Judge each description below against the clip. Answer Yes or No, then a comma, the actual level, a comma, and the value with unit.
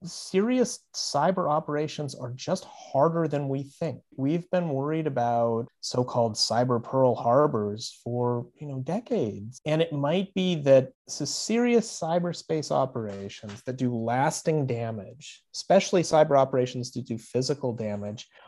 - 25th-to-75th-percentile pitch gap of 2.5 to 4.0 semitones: No, wide, 5.4 semitones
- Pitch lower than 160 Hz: Yes, medium, 140 Hz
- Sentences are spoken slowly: Yes, slow, 130 wpm